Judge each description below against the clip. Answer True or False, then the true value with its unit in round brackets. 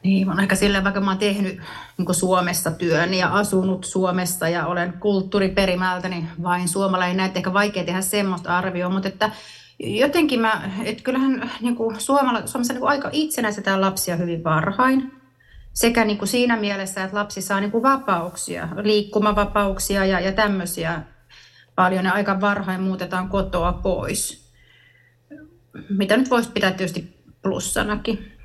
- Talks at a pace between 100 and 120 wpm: False (135 wpm)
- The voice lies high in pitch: True (195 Hz)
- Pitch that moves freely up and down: False (2.7 semitones)